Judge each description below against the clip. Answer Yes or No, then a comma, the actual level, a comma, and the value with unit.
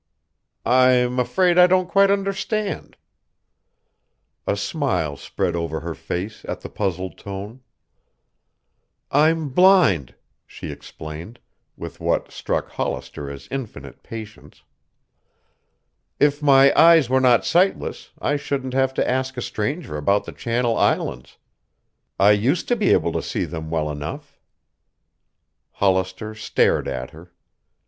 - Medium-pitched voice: No, low, 120 Hz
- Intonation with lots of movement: Yes, wide, 8.6 semitones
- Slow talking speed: Yes, slow, 125 wpm